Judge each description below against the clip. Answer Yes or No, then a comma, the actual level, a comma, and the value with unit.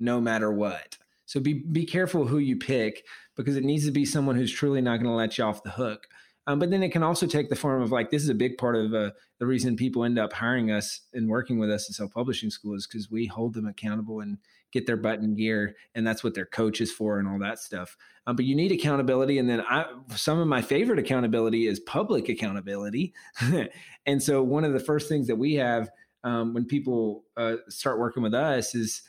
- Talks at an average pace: No, fast, 240 wpm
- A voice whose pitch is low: Yes, low, 120 Hz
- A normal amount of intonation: Yes, average, 4.2 semitones